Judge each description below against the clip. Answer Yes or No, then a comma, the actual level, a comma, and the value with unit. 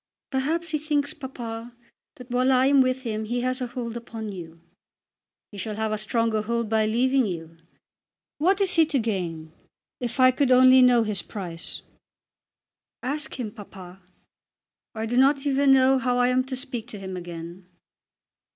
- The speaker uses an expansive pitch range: No, average, 3.6 semitones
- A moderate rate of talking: Yes, average, 170 wpm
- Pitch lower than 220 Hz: No, high, 245 Hz